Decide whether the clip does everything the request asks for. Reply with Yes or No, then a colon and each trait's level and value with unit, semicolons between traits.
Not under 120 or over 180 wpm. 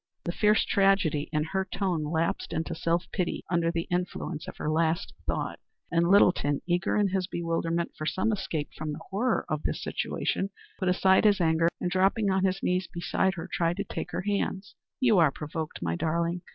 No: average, 190 wpm